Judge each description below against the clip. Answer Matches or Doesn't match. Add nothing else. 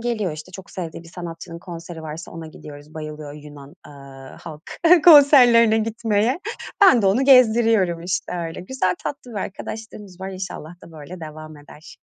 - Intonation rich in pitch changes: Matches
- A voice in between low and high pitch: Matches